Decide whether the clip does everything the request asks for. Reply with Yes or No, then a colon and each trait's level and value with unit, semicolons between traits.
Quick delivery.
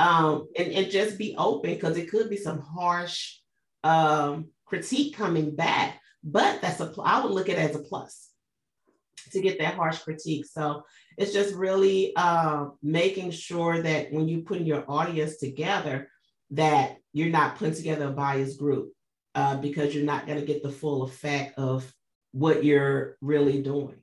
No: average, 175 wpm